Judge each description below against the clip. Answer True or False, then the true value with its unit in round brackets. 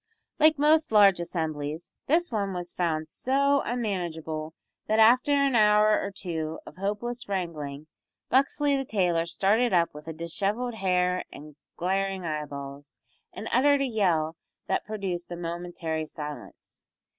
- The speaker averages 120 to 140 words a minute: True (135 wpm)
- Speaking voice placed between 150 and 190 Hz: True (185 Hz)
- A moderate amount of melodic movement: False (5.9 semitones)